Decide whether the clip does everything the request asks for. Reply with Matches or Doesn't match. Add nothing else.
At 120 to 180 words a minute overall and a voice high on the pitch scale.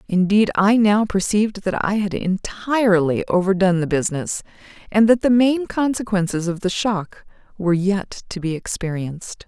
Matches